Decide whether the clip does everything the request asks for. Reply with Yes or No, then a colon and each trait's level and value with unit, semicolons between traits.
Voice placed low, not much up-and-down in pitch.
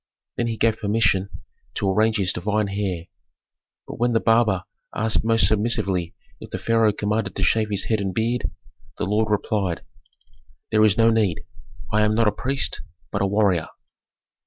Yes: low, 105 Hz; narrow, 2.2 semitones